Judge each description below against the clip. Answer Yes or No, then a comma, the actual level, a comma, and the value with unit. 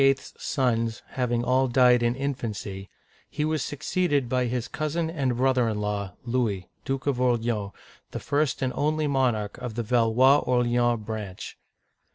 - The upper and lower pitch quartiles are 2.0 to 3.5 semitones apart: Yes, average, 3.0 semitones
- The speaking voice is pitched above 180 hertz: No, low, 125 Hz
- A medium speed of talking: Yes, average, 155 wpm